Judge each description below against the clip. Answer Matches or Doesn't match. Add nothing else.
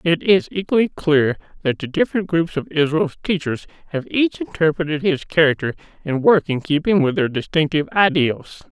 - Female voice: Doesn't match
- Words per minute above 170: Doesn't match